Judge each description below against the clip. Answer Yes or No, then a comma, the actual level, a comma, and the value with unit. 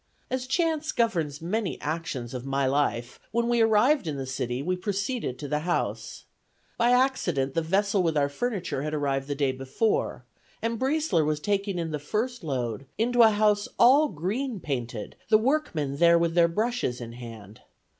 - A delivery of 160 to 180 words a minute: Yes, average, 175 wpm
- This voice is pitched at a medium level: Yes, medium, 170 Hz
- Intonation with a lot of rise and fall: Yes, wide, 8.6 semitones